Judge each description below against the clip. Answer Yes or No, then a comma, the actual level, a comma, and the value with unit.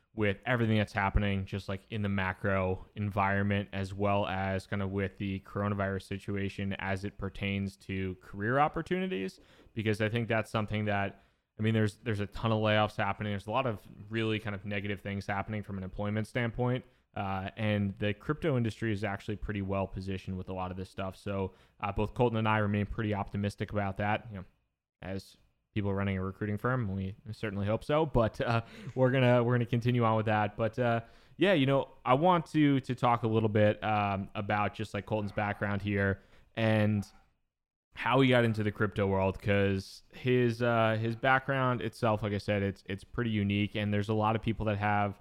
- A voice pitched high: No, low, 105 Hz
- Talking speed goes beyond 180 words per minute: Yes, average, 200 wpm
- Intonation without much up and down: Yes, narrow, 2.3 semitones